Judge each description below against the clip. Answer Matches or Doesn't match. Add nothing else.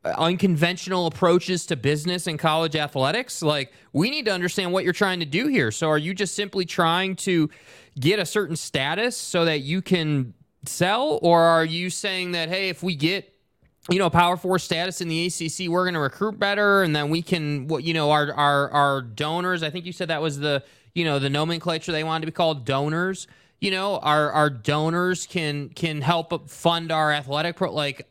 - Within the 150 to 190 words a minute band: Doesn't match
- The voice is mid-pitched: Matches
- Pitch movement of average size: Matches